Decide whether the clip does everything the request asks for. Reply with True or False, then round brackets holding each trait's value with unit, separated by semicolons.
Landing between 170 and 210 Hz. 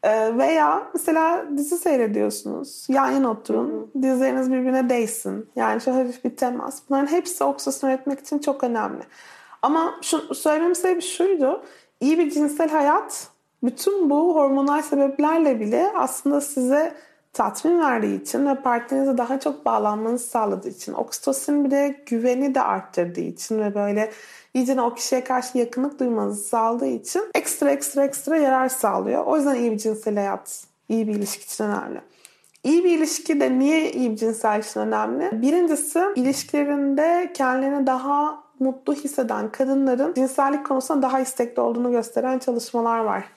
False (270 Hz)